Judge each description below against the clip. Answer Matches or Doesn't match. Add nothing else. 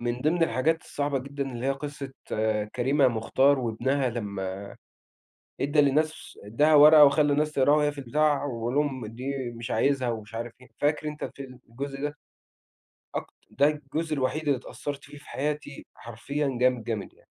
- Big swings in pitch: Doesn't match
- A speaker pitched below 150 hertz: Matches